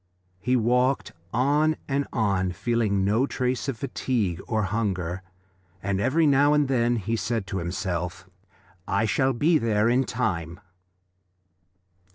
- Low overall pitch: Yes, low, 115 Hz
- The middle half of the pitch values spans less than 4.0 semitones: No, average, 5.3 semitones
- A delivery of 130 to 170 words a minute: Yes, slow, 135 wpm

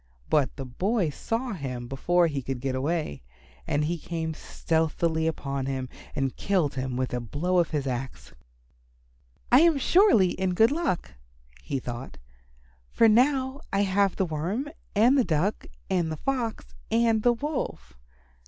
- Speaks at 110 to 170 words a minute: Yes, average, 155 wpm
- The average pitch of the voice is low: No, medium, 170 Hz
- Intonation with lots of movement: Yes, wide, 8.5 semitones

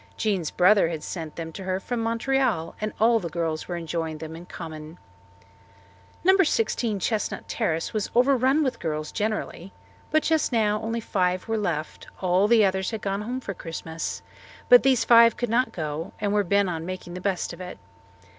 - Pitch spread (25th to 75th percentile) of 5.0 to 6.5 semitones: Yes, wide, 5.4 semitones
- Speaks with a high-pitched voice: Yes, high, 195 Hz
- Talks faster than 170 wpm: Yes, average, 185 wpm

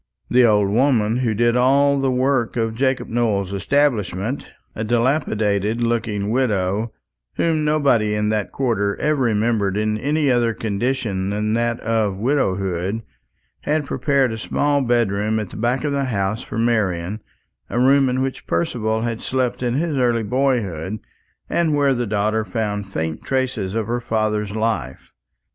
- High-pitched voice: No, low, 115 Hz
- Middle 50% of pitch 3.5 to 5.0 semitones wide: Yes, average, 3.8 semitones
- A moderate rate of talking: Yes, average, 155 wpm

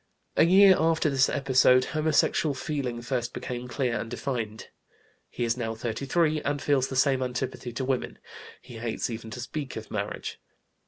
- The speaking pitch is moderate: No, low, 130 Hz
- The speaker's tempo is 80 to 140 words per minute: No, average, 165 wpm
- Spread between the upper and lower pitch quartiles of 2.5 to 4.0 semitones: Yes, average, 3.2 semitones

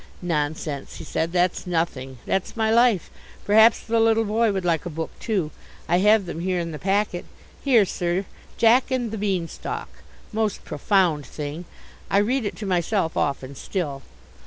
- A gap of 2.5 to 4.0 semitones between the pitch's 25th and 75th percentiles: No, average, 5.0 semitones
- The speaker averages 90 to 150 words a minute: No, average, 170 wpm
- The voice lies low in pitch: No, medium, 185 Hz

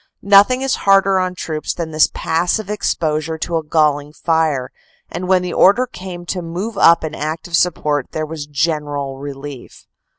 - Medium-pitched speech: Yes, medium, 160 Hz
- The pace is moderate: Yes, average, 165 wpm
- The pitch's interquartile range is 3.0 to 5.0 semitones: Yes, average, 3.5 semitones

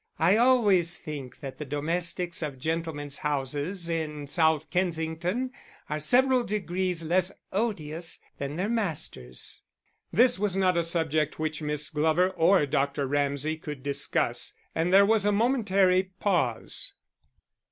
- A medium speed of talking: No, slow, 130 wpm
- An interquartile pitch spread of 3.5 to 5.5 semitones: Yes, average, 4.1 semitones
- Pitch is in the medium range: Yes, medium, 165 Hz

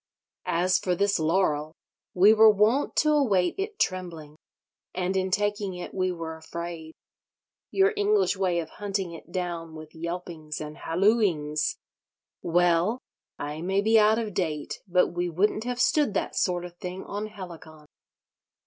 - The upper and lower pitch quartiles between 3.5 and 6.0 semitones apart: Yes, average, 3.9 semitones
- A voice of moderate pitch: Yes, medium, 180 Hz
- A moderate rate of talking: Yes, average, 150 wpm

